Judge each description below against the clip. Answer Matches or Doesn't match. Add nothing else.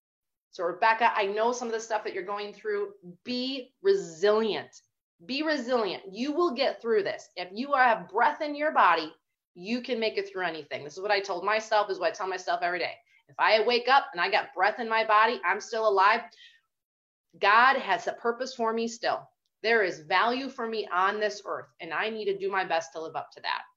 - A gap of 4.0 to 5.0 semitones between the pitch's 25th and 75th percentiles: Matches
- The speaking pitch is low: Doesn't match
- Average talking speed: Doesn't match